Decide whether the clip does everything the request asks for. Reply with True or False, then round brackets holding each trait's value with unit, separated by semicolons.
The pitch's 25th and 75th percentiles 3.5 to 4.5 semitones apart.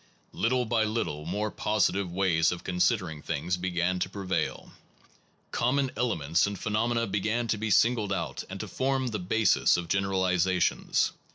True (3.9 semitones)